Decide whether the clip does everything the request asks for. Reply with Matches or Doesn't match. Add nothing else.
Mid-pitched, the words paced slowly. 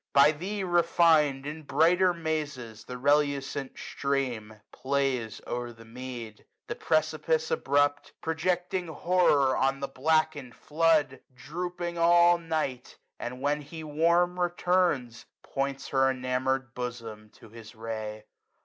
Matches